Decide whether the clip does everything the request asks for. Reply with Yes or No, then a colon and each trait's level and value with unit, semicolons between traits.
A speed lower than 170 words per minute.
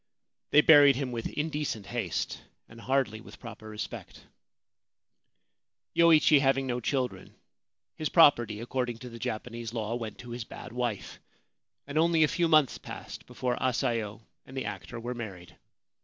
Yes: average, 150 wpm